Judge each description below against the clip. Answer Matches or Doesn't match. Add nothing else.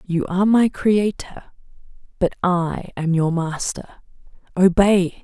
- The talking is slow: Matches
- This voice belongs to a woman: Matches